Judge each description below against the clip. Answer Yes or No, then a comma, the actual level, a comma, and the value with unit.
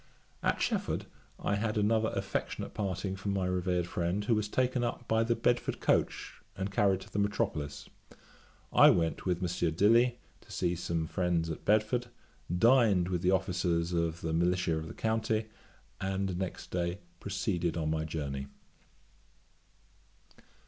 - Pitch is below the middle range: Yes, very low, 95 Hz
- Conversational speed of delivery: Yes, average, 150 wpm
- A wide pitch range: No, average, 3.8 semitones